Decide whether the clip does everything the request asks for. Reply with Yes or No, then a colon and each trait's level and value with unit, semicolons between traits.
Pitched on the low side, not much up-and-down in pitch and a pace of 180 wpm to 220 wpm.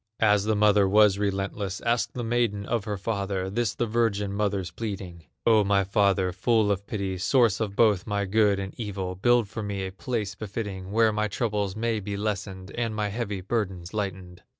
Yes: low, 100 Hz; narrow, 2.2 semitones; average, 190 wpm